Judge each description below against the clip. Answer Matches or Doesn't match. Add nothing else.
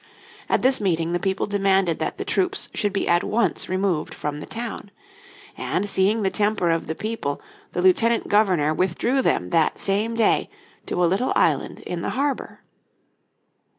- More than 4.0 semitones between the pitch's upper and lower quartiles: Matches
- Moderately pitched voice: Doesn't match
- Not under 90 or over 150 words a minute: Doesn't match